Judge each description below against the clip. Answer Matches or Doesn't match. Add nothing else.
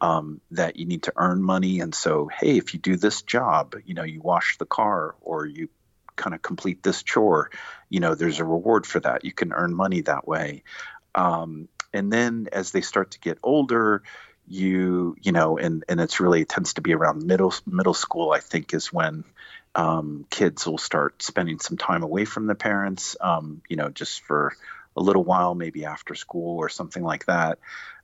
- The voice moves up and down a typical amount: Matches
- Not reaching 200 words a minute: Doesn't match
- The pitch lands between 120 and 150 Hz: Doesn't match